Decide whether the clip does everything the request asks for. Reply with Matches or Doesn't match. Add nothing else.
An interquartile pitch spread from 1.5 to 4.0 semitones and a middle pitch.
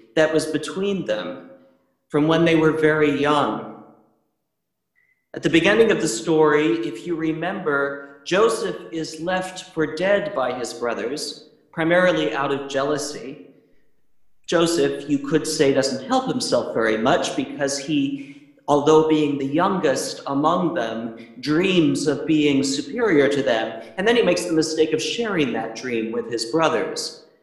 Matches